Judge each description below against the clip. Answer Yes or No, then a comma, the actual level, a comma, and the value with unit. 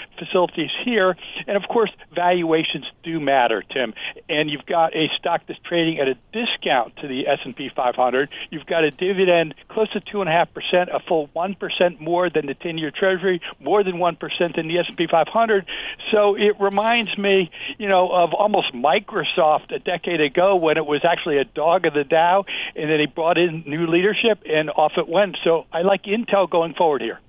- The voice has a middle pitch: Yes, medium, 175 Hz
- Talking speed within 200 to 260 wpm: Yes, fast, 205 wpm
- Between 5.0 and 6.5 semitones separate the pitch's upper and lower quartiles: No, average, 3.6 semitones